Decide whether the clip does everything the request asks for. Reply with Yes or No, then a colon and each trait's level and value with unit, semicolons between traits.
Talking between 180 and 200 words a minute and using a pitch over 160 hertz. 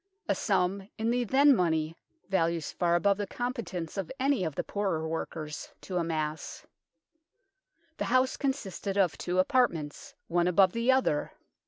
No: average, 150 wpm; high, 190 Hz